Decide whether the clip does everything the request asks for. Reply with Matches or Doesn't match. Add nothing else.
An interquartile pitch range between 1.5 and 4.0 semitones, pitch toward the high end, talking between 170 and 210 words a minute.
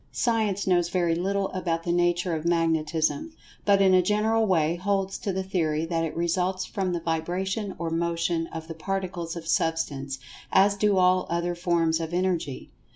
Doesn't match